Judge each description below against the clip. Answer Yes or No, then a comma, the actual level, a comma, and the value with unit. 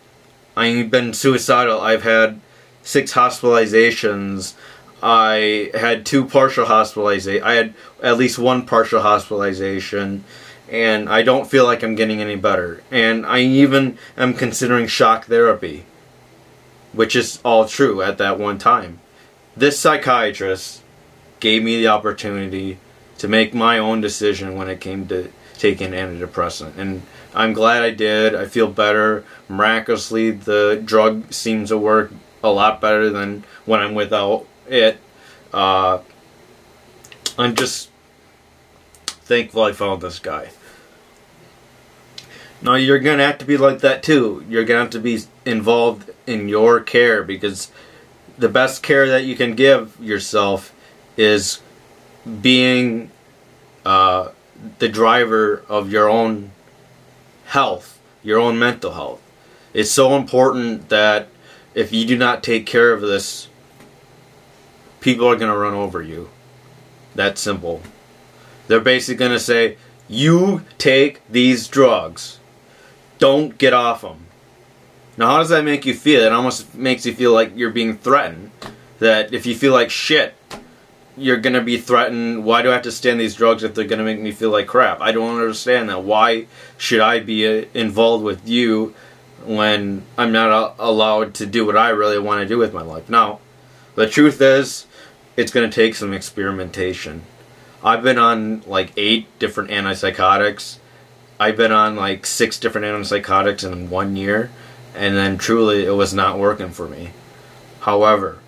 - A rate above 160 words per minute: No, average, 150 wpm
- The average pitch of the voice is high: No, low, 110 Hz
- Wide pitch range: No, average, 2.8 semitones